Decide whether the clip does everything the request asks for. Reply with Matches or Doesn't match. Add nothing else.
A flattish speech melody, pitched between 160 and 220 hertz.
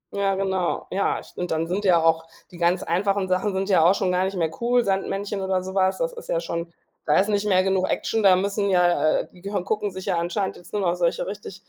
Matches